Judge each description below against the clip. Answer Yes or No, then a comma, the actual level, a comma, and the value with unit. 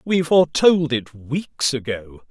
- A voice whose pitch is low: No, medium, 145 Hz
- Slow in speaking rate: Yes, slow, 130 wpm